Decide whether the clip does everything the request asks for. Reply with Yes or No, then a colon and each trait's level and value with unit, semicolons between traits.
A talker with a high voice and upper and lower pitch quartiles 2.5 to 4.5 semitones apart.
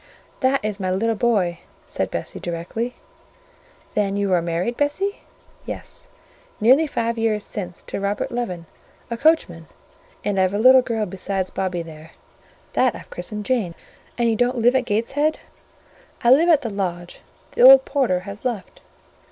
No: high, 215 Hz; average, 5.1 semitones